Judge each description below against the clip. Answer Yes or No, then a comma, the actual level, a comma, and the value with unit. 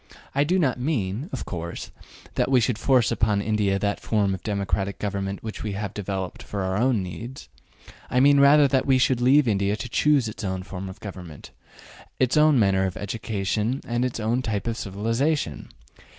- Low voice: Yes, low, 110 Hz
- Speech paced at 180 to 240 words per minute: Yes, average, 190 wpm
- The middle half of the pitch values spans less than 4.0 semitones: No, average, 4.7 semitones